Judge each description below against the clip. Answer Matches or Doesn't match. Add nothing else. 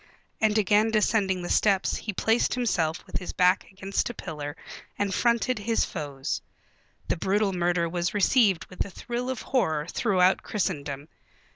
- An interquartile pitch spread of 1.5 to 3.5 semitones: Doesn't match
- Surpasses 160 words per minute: Doesn't match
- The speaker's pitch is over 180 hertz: Matches